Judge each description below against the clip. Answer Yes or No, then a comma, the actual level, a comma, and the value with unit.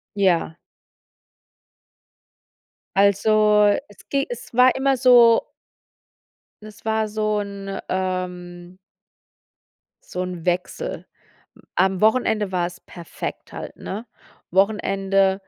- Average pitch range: Yes, average, 3.0 semitones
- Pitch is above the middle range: Yes, high, 200 Hz